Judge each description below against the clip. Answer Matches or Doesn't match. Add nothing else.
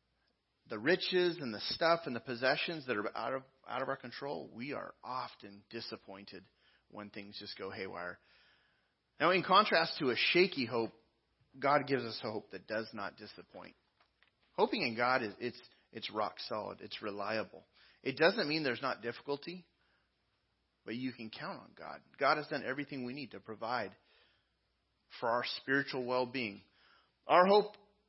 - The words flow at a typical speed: Matches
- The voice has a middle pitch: Doesn't match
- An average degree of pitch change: Matches